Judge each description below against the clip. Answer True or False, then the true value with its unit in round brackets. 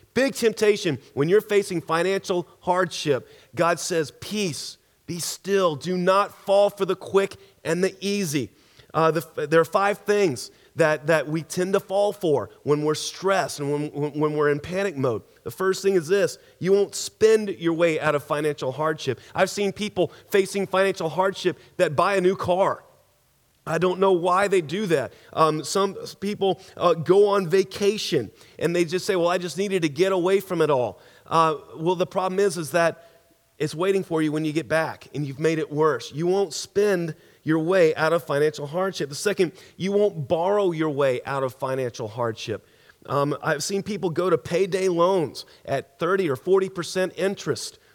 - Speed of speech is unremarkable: True (190 wpm)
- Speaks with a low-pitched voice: False (175 Hz)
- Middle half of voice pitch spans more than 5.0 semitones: False (3.7 semitones)